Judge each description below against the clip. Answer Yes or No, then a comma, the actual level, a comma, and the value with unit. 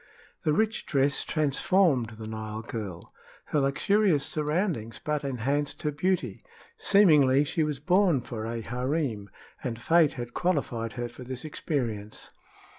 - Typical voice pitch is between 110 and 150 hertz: Yes, medium, 140 Hz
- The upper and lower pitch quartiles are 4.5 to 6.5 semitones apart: Yes, average, 5.0 semitones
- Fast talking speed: No, slow, 135 wpm